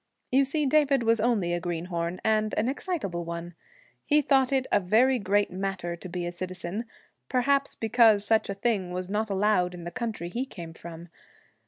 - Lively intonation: Yes, wide, 5.7 semitones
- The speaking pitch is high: Yes, high, 205 Hz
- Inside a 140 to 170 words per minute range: No, average, 185 wpm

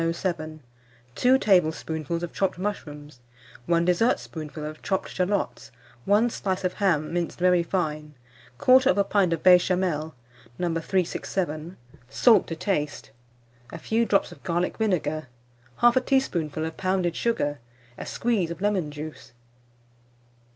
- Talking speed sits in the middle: No, slow, 125 wpm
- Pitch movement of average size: Yes, average, 4.0 semitones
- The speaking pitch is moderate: Yes, medium, 175 Hz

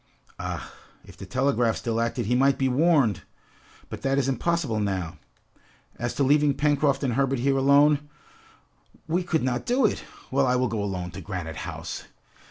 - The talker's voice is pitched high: No, low, 135 Hz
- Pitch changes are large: No, average, 3.8 semitones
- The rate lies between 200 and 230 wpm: No, average, 175 wpm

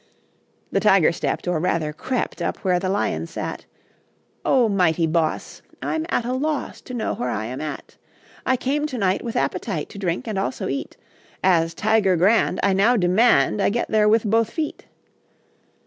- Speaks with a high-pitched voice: Yes, high, 195 Hz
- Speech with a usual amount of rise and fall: No, wide, 5.7 semitones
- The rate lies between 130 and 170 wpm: No, average, 180 wpm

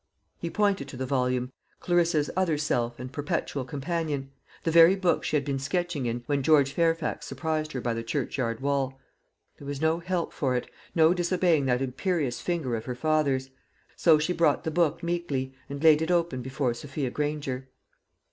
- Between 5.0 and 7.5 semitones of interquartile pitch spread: No, average, 4.1 semitones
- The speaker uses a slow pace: No, average, 180 wpm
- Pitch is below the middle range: No, medium, 145 Hz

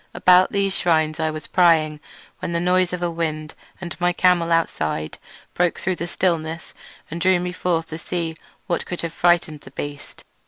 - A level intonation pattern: Yes, narrow, 2.0 semitones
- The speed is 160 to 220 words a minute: Yes, average, 190 wpm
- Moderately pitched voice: Yes, medium, 170 Hz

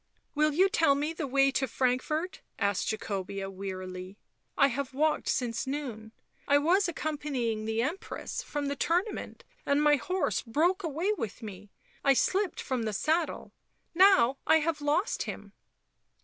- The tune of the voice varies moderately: No, wide, 5.9 semitones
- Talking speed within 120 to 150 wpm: No, average, 165 wpm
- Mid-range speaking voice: No, very high, 280 Hz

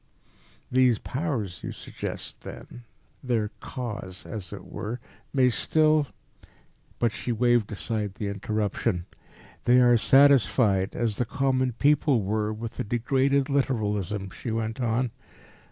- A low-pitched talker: Yes, low, 115 Hz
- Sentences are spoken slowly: Yes, slow, 130 wpm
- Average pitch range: Yes, average, 3.5 semitones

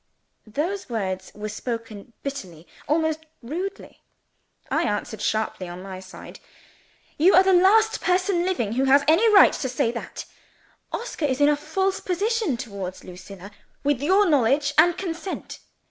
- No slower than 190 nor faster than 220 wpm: No, average, 145 wpm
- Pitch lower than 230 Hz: No, very high, 290 Hz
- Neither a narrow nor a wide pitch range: No, wide, 8.9 semitones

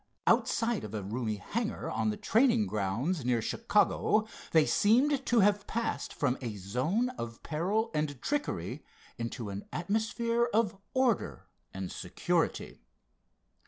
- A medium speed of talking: No, slow, 130 wpm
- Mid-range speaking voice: Yes, medium, 180 Hz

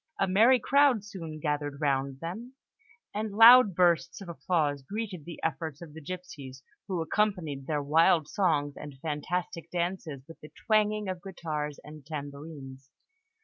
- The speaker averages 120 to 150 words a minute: Yes, average, 145 wpm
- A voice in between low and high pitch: Yes, medium, 165 Hz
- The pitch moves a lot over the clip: No, average, 4.8 semitones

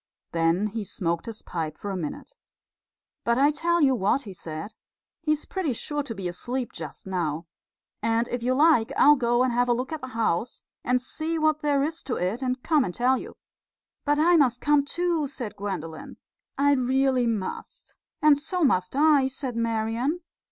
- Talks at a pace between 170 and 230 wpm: Yes, average, 185 wpm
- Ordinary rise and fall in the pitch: No, wide, 5.7 semitones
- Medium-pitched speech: No, very high, 250 Hz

